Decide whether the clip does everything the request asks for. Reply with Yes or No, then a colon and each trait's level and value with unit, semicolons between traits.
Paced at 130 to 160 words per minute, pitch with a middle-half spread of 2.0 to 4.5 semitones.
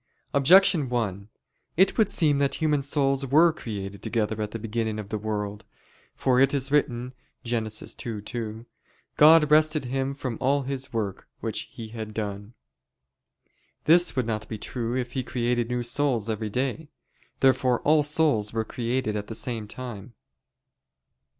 Yes: average, 155 wpm; average, 4.1 semitones